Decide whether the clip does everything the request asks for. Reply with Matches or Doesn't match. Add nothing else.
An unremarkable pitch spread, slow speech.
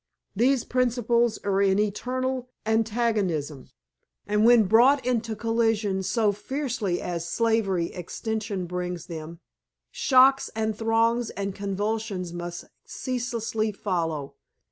Matches